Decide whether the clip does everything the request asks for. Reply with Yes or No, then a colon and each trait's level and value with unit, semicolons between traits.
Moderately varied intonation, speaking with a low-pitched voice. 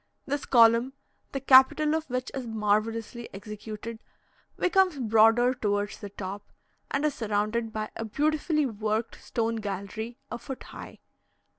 No: average, 3.8 semitones; high, 230 Hz